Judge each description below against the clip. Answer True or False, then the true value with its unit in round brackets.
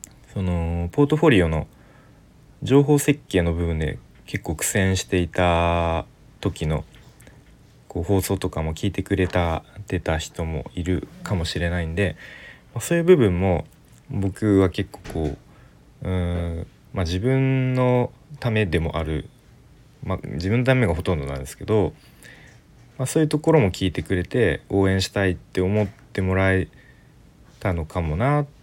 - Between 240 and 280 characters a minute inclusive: True (275 characters per minute)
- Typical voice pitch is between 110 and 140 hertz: False (95 Hz)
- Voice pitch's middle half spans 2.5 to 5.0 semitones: False (5.4 semitones)